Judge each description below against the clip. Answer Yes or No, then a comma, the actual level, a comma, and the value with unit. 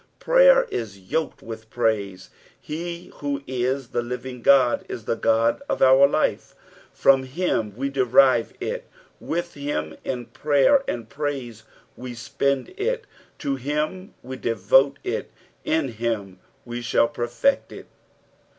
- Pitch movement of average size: Yes, average, 4.0 semitones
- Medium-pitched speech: No, low, 130 Hz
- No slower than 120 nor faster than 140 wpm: Yes, slow, 135 wpm